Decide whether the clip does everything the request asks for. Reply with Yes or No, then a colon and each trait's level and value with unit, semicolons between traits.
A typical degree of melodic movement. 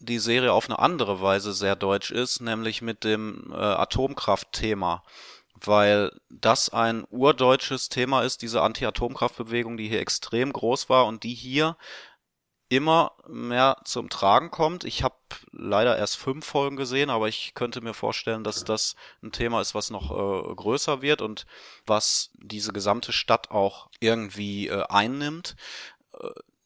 Yes: average, 3.6 semitones